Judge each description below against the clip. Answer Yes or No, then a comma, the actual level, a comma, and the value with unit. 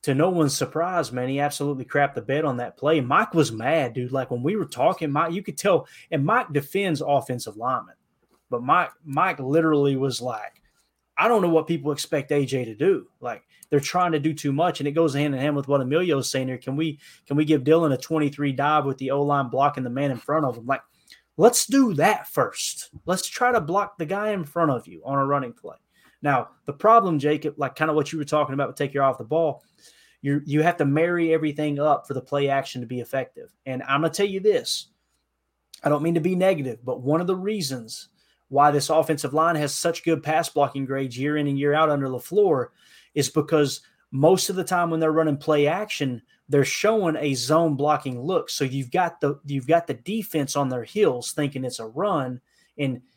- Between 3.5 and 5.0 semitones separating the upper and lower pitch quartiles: No, average, 3.0 semitones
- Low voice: No, medium, 145 Hz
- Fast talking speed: Yes, fast, 230 wpm